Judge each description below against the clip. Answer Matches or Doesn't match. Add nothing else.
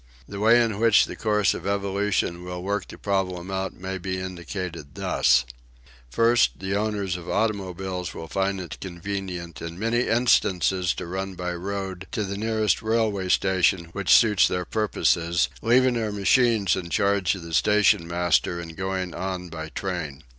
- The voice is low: Matches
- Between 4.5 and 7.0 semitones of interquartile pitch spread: Doesn't match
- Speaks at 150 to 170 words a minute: Matches